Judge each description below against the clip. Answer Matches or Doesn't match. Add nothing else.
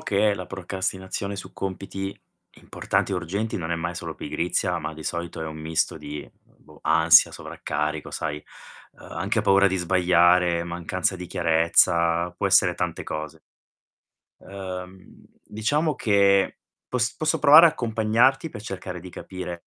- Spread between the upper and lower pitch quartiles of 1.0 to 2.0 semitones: Doesn't match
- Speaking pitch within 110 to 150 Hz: Doesn't match